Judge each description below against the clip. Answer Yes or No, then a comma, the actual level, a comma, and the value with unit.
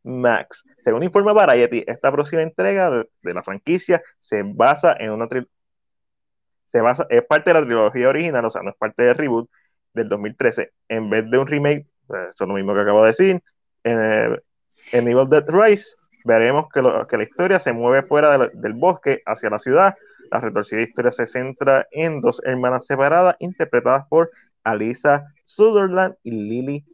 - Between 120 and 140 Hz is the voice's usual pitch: Yes, low, 135 Hz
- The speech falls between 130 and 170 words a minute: No, average, 185 wpm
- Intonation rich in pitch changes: Yes, wide, 5.7 semitones